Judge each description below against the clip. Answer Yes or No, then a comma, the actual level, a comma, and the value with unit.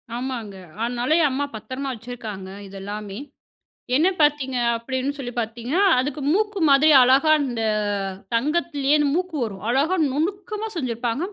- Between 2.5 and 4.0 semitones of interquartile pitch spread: No, average, 4.6 semitones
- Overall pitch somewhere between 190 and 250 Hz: No, very high, 260 Hz